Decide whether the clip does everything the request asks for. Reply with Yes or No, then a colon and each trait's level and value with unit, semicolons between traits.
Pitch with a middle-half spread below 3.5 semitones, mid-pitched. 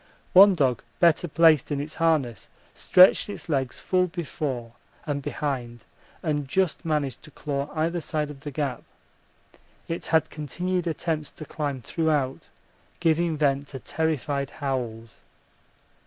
Yes: average, 3.1 semitones; medium, 150 Hz